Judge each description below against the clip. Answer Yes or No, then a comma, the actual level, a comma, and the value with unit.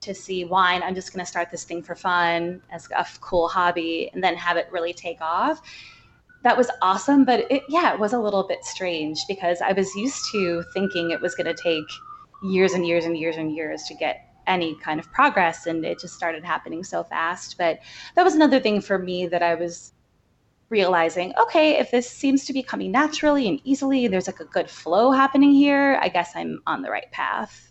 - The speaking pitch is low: No, medium, 185 Hz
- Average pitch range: No, wide, 7.8 semitones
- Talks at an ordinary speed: No, fast, 215 wpm